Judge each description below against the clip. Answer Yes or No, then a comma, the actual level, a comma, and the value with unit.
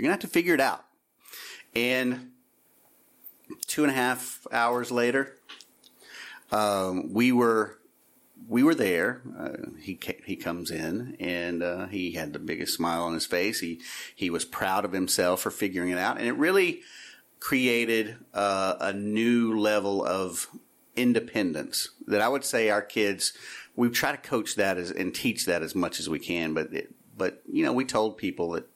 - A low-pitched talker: Yes, low, 110 Hz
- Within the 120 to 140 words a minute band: No, average, 175 wpm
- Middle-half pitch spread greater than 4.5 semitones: Yes, average, 5.0 semitones